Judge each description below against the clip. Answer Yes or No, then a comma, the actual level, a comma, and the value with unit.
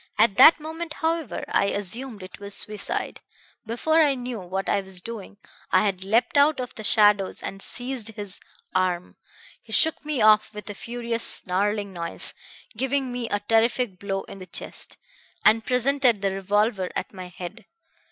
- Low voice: No, high, 215 Hz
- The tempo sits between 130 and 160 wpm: No, average, 170 wpm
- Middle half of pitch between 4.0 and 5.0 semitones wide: Yes, average, 4.3 semitones